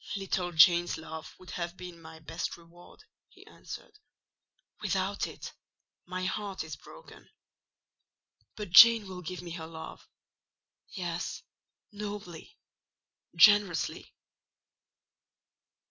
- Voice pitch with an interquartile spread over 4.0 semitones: No, average, 2.8 semitones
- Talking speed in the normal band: No, slow, 100 wpm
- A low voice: No, medium, 175 Hz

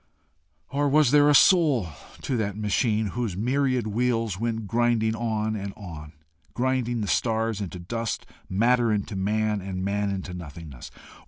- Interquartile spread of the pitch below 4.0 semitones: Yes, average, 3.4 semitones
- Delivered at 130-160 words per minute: Yes, average, 150 wpm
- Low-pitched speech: Yes, low, 110 Hz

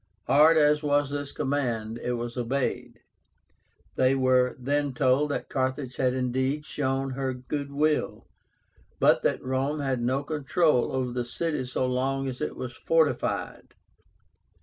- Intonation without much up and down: Yes, narrow, 2.3 semitones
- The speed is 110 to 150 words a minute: Yes, average, 145 wpm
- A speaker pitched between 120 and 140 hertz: Yes, low, 135 Hz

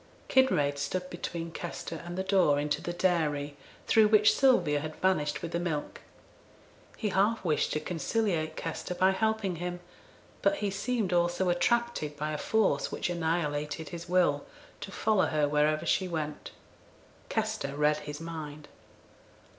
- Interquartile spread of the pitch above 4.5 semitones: No, average, 4.0 semitones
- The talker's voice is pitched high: No, medium, 170 Hz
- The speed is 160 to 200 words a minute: No, average, 150 wpm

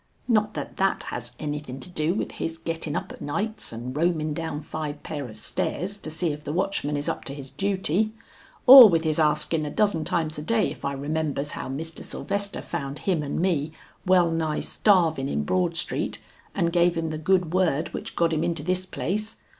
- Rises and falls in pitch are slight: No, average, 3.8 semitones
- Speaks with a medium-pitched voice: Yes, medium, 160 Hz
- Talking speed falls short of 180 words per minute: No, fast, 205 wpm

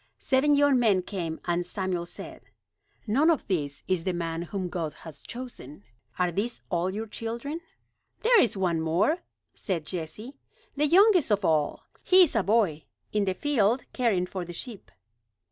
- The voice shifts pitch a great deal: Yes, wide, 6.6 semitones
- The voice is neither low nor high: No, high, 195 Hz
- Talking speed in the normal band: Yes, average, 165 wpm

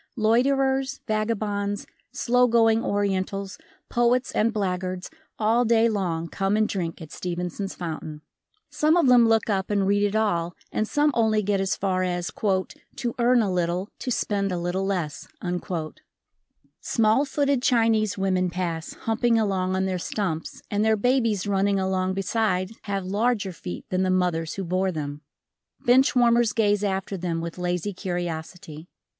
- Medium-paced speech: Yes, average, 155 wpm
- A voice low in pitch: No, high, 200 Hz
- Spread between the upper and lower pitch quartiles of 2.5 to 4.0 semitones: Yes, average, 3.6 semitones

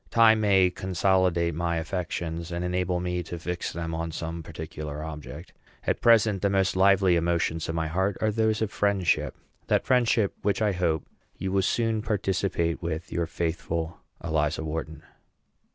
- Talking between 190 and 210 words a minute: No, average, 155 wpm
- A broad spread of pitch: No, average, 3.1 semitones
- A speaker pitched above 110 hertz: No, very low, 85 Hz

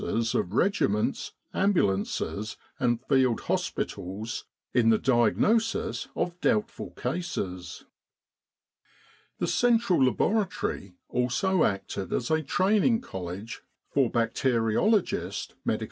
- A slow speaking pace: Yes, slow, 95 wpm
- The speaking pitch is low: Yes, low, 125 Hz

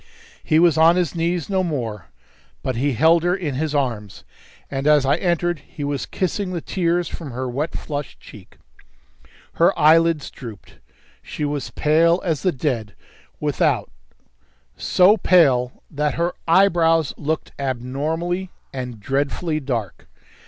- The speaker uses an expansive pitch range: No, average, 4.2 semitones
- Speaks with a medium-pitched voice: Yes, medium, 155 Hz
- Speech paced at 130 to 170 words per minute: Yes, average, 140 wpm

